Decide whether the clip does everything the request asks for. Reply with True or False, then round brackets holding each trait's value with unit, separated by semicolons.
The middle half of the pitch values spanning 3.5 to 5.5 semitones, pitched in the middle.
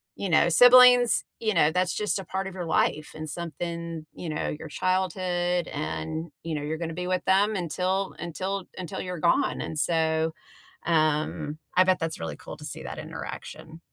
False (2.7 semitones; 170 Hz)